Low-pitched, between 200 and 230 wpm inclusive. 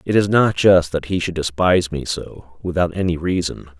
Yes: very low, 90 Hz; fast, 205 wpm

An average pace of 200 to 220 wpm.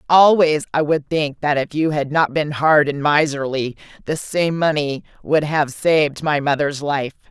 No: average, 180 wpm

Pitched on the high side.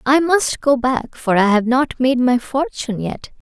Yes: very high, 255 Hz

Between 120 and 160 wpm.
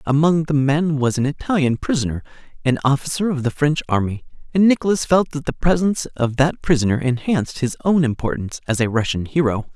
No: average, 185 wpm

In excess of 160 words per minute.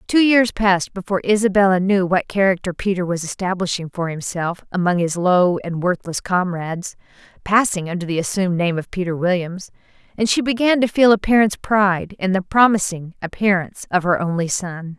Yes: average, 170 wpm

